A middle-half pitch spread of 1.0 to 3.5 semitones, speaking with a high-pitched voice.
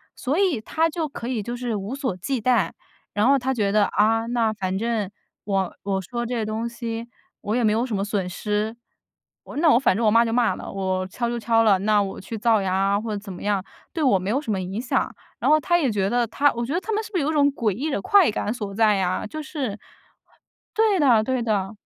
No: average, 4.1 semitones; high, 225 Hz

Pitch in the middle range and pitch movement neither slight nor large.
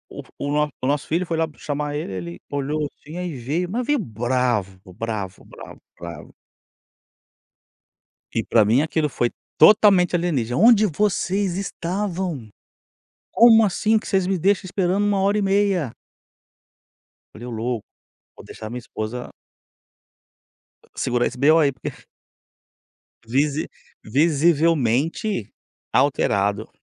No: medium, 150 Hz; wide, 7.6 semitones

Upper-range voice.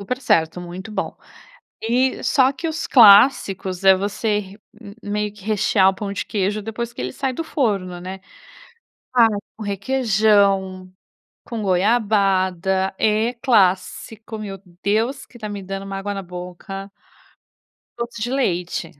Yes: high, 205 Hz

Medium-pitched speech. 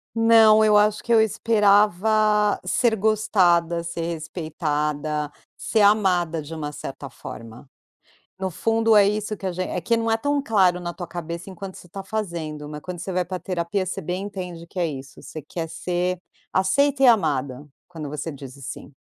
Yes: medium, 180 Hz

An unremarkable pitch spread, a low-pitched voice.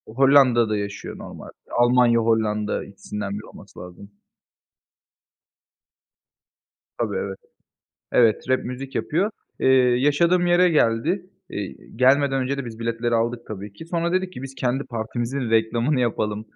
Yes: average, 3.8 semitones; low, 120 Hz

